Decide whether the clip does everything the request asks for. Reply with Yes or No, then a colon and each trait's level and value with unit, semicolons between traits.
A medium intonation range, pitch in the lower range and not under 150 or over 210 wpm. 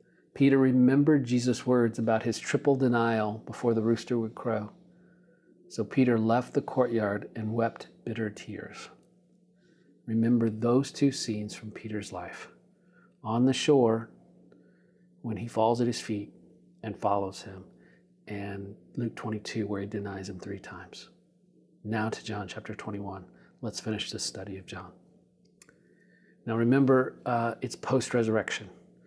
No: average, 3.4 semitones; low, 115 Hz; average, 140 wpm